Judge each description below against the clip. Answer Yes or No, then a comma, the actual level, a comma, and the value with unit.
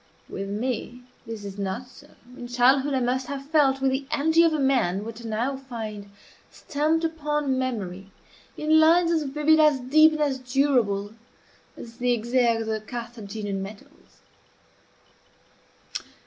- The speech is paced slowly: No, average, 150 wpm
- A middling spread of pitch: Yes, average, 4.7 semitones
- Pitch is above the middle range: Yes, very high, 255 Hz